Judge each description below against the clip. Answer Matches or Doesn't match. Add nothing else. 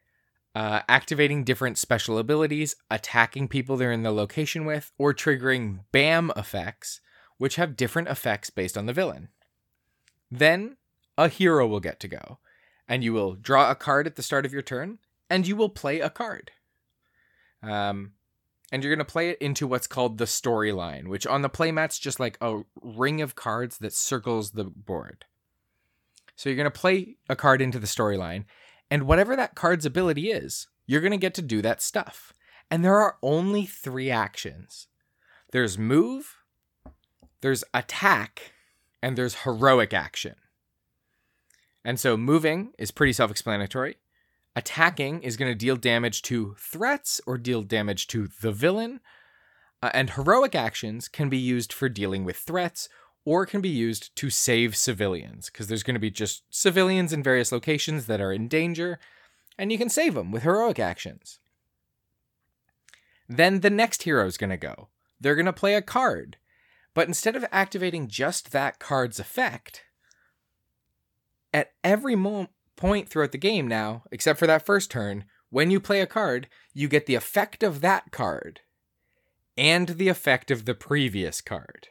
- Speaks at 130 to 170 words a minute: Matches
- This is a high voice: Doesn't match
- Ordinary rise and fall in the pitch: Doesn't match